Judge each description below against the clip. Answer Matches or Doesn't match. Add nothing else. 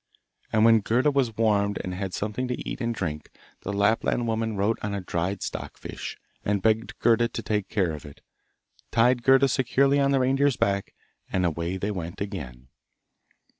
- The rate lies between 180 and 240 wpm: Matches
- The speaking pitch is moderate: Doesn't match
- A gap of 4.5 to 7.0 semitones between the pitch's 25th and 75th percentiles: Doesn't match